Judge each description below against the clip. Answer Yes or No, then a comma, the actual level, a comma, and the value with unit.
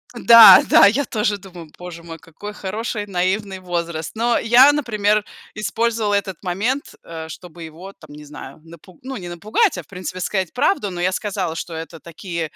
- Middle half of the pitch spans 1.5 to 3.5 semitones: No, average, 4.1 semitones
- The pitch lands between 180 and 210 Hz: Yes, high, 190 Hz